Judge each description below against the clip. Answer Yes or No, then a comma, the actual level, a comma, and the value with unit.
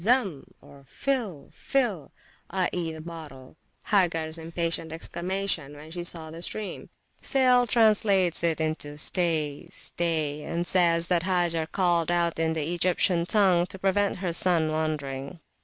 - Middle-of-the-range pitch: Yes, medium, 170 Hz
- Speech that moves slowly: Yes, slow, 130 wpm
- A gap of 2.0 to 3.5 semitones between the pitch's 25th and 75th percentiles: Yes, average, 2.9 semitones